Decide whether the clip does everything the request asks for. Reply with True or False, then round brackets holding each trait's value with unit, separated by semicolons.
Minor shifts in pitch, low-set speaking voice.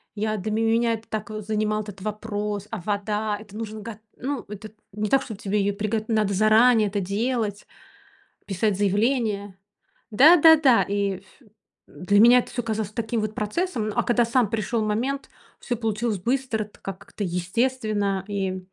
False (2.2 semitones; 215 Hz)